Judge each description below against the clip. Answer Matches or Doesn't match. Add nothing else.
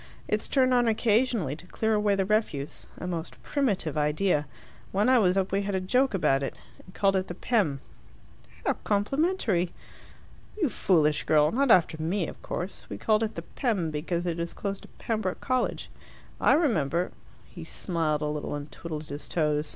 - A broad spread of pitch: Matches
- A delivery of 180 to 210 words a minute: Matches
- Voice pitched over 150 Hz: Matches